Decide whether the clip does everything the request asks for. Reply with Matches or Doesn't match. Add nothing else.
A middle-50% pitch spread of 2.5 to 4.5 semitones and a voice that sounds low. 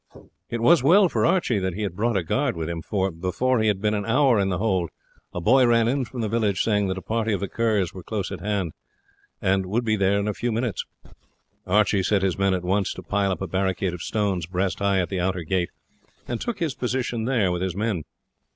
Matches